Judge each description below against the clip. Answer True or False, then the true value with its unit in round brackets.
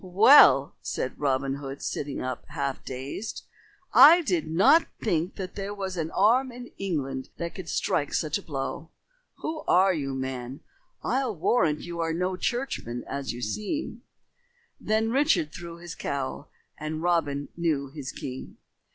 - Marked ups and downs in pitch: True (6.3 semitones)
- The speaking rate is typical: True (150 wpm)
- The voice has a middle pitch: True (165 Hz)